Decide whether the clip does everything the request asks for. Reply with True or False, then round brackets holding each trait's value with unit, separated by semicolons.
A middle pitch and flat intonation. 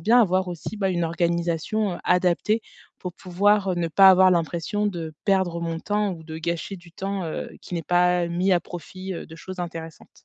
True (180 Hz; 2.2 semitones)